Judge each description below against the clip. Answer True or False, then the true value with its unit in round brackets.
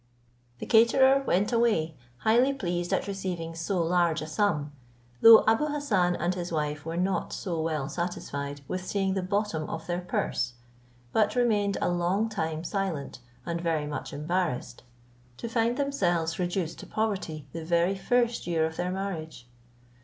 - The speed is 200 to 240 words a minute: False (160 wpm)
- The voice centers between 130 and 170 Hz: False (180 Hz)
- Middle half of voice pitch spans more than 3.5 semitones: True (4.4 semitones)